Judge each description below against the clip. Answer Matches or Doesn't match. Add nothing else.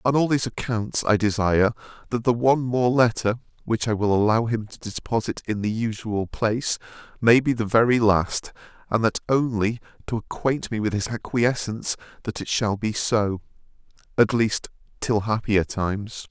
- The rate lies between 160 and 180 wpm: Matches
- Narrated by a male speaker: Matches